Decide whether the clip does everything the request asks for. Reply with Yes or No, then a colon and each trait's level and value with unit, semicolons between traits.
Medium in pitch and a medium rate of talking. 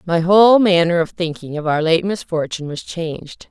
Yes: medium, 170 Hz; average, 190 wpm